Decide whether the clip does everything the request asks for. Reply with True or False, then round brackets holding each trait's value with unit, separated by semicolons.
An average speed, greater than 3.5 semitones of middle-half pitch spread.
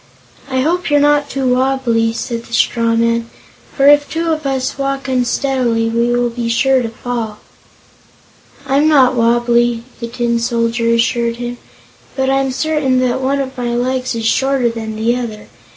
False (165 wpm; 2.5 semitones)